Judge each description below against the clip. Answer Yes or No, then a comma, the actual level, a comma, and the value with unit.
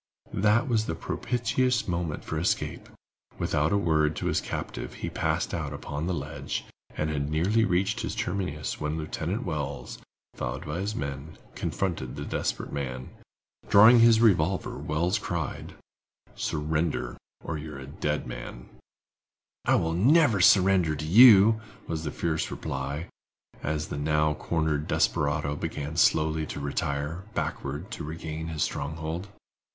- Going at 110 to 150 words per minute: Yes, average, 145 wpm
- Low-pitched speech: Yes, very low, 80 Hz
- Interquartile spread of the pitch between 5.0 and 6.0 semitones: No, average, 4.3 semitones